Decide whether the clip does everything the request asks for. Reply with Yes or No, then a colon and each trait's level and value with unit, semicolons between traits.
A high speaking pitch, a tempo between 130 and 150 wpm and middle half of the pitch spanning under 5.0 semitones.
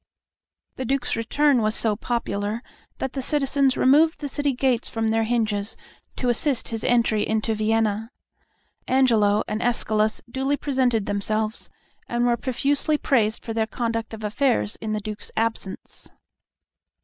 Yes: high, 230 Hz; average, 145 wpm; average, 3.4 semitones